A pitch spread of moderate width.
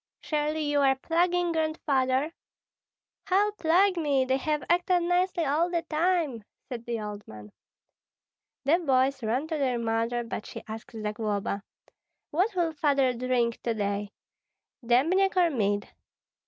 No: wide, 6.3 semitones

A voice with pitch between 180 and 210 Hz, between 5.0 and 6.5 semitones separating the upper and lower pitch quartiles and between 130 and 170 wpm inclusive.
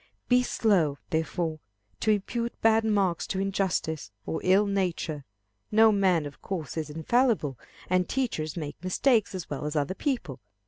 Yes: medium, 185 Hz; wide, 5.5 semitones; average, 150 wpm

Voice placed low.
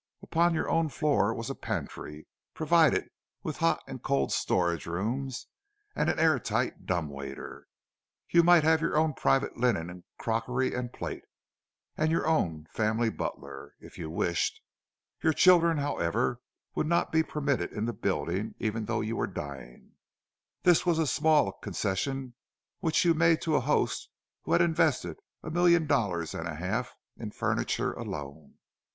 Yes: low, 125 Hz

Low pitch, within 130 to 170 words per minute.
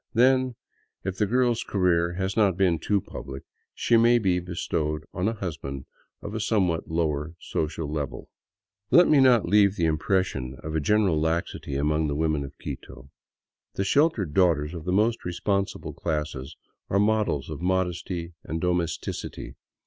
Yes: very low, 90 Hz; average, 155 wpm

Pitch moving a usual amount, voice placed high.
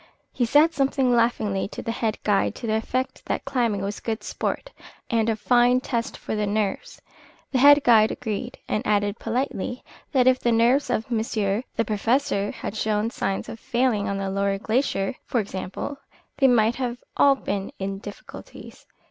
Yes: average, 3.5 semitones; high, 225 Hz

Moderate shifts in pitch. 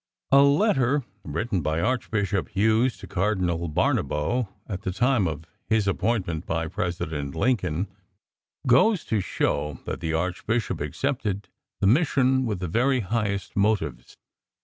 No: wide, 6.2 semitones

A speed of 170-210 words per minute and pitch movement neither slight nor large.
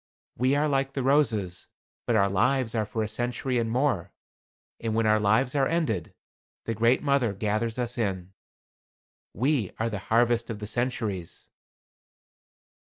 No: average, 155 wpm; average, 3.3 semitones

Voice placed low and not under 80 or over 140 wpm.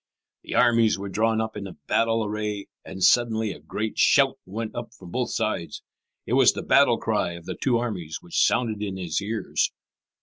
No: low, 110 Hz; average, 190 wpm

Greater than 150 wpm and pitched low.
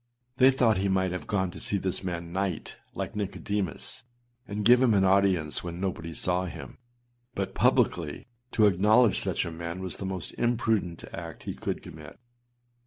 Yes: average, 175 wpm; very low, 95 Hz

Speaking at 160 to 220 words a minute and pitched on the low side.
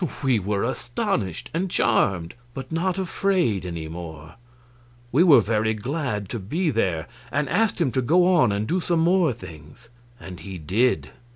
Yes: average, 165 wpm; low, 120 Hz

